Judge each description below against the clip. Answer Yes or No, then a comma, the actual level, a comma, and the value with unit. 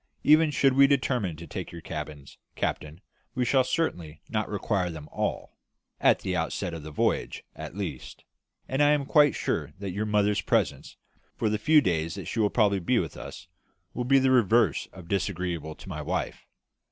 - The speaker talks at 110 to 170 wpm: No, average, 190 wpm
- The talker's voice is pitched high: No, low, 100 Hz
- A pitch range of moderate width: No, wide, 7.4 semitones